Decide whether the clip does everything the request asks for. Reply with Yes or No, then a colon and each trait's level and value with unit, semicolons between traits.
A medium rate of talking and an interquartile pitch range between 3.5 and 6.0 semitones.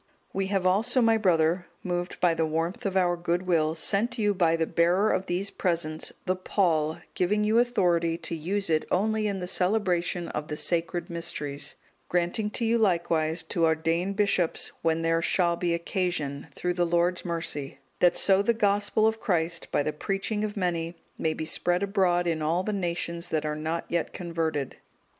No: average, 185 wpm; average, 3.0 semitones